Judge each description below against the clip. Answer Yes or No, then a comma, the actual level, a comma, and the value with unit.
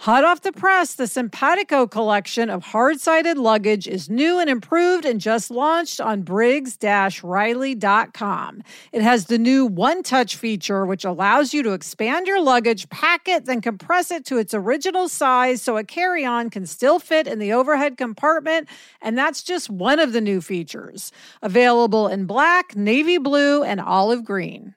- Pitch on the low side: No, high, 245 Hz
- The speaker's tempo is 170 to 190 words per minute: No, average, 160 wpm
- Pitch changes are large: Yes, wide, 6.6 semitones